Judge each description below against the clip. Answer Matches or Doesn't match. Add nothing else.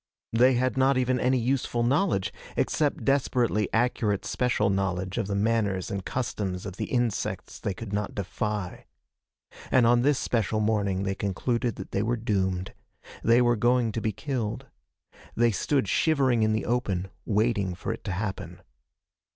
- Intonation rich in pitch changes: Doesn't match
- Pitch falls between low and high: Doesn't match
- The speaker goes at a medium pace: Matches